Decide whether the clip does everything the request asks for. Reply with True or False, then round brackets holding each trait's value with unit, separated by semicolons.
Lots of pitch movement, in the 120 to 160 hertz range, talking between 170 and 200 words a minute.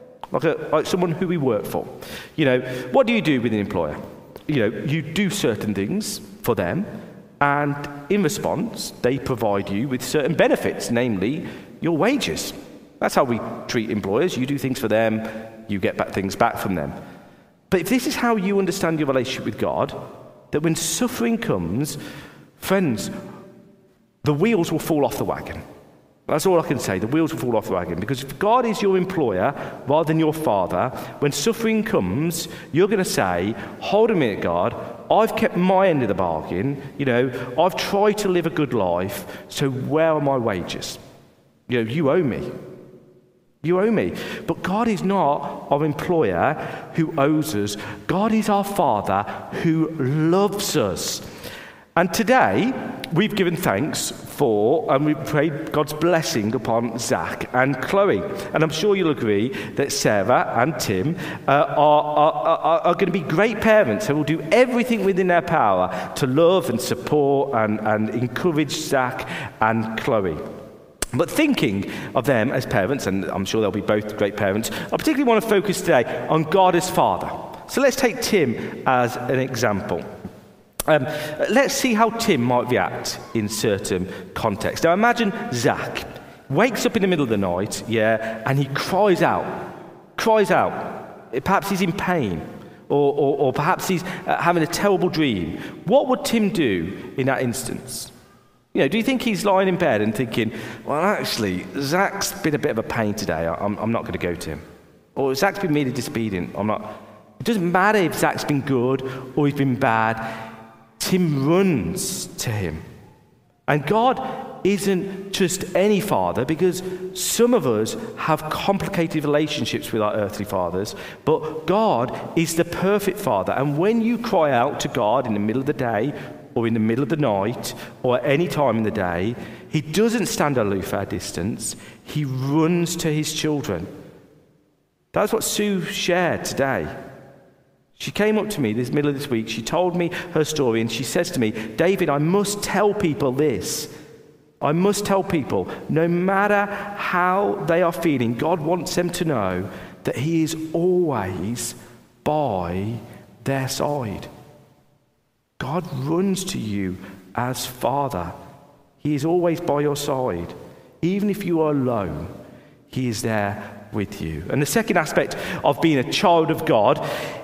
True (7.5 semitones; 155 Hz; 175 wpm)